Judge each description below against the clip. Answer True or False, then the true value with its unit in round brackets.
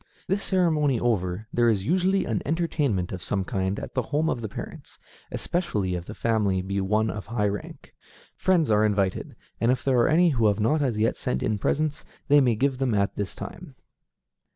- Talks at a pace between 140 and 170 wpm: False (200 wpm)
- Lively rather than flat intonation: True (6.5 semitones)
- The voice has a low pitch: True (115 Hz)